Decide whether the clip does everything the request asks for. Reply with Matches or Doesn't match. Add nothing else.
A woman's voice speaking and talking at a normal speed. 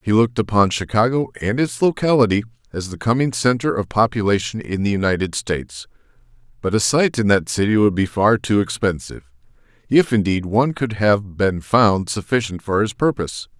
Doesn't match